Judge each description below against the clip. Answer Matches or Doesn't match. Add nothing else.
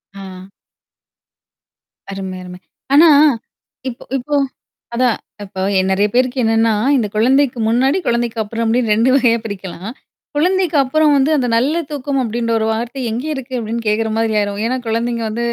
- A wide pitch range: Doesn't match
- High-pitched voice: Matches